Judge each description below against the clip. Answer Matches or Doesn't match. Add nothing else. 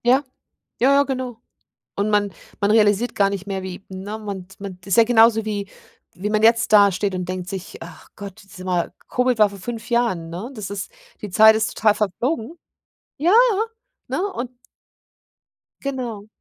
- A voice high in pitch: Matches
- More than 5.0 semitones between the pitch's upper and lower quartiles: Doesn't match